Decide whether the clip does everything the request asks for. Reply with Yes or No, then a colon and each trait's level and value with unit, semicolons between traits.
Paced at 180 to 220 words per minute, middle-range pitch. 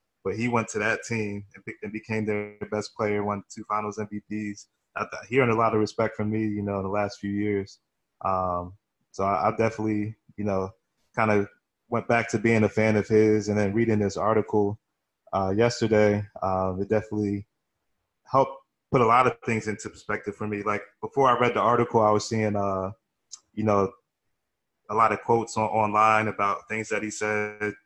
No: average, 190 wpm; low, 105 Hz